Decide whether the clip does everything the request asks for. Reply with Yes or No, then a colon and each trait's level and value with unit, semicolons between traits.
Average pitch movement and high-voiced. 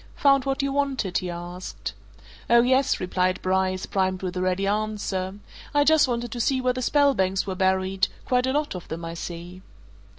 No: wide, 5.9 semitones; high, 195 Hz